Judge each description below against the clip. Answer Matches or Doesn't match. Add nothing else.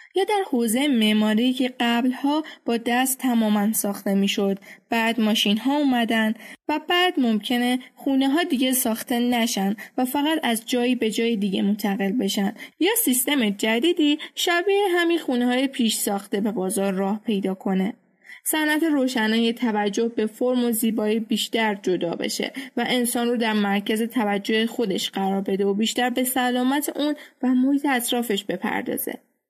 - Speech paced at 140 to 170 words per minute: Matches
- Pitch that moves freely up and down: Doesn't match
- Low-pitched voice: Doesn't match